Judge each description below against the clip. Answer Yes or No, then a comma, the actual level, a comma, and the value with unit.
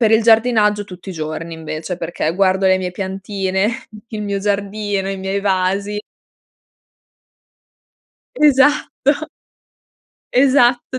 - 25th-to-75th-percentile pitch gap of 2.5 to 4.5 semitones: Yes, average, 2.8 semitones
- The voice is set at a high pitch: Yes, high, 200 Hz